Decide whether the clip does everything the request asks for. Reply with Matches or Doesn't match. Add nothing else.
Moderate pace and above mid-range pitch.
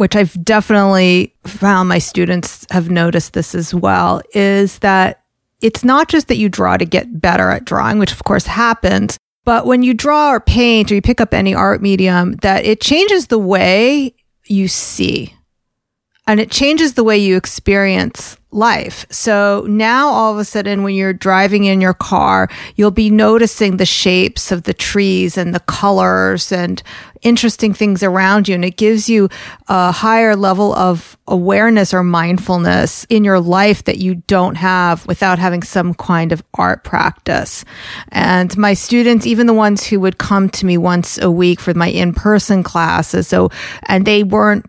Matches